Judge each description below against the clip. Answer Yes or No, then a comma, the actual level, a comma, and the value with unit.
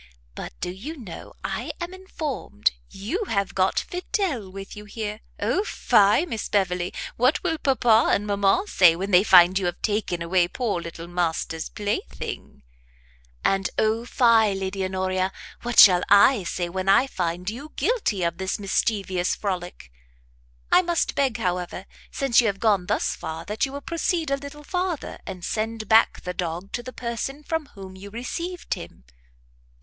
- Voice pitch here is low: No, high, 205 Hz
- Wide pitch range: Yes, wide, 5.8 semitones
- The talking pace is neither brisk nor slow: Yes, average, 165 wpm